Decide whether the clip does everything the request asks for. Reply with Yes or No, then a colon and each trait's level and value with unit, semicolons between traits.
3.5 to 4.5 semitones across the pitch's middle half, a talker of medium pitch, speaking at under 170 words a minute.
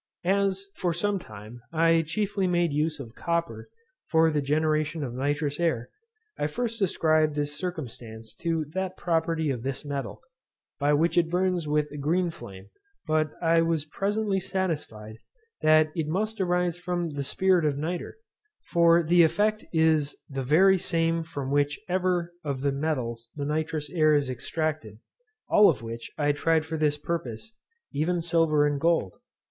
No: average, 3.1 semitones; medium, 160 Hz; average, 160 wpm